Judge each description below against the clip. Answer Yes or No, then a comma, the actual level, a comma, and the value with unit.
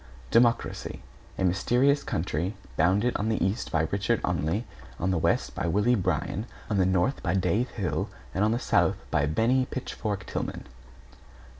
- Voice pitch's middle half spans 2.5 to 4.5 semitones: No, average, 4.9 semitones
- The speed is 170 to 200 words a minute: No, average, 160 wpm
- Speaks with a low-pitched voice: Yes, low, 100 Hz